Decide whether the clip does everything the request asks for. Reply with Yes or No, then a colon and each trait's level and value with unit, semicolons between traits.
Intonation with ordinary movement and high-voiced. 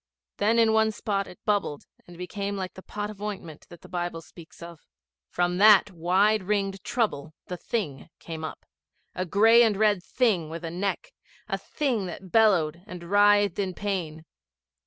Yes: average, 3.4 semitones; high, 195 Hz